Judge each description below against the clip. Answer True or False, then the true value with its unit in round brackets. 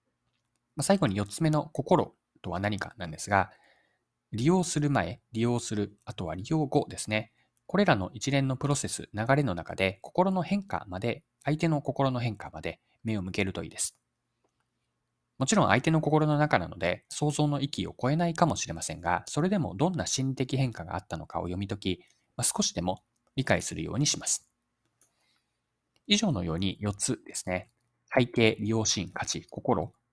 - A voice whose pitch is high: False (115 Hz)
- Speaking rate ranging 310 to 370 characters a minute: True (325 characters per minute)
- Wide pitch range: True (7.2 semitones)